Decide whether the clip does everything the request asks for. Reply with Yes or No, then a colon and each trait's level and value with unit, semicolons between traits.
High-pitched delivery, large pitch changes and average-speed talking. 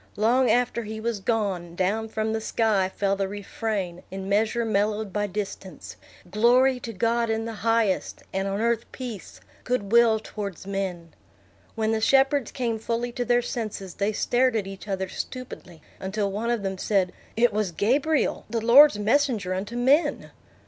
No: high, 220 Hz; average, 3.1 semitones; average, 170 wpm